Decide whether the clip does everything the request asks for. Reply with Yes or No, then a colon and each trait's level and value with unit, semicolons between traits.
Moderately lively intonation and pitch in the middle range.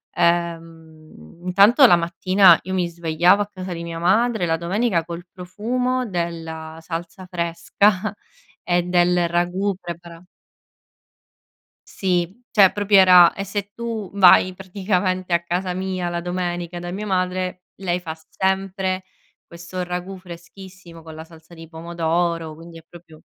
No: narrow, 2.0 semitones; medium, 180 Hz